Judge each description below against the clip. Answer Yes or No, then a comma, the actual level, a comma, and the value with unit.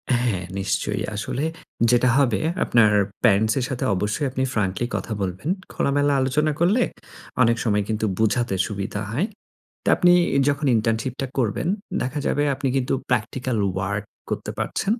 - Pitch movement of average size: Yes, average, 4.5 semitones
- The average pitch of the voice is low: Yes, low, 120 Hz